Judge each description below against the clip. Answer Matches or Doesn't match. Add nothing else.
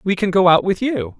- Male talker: Matches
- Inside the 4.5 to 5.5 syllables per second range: Matches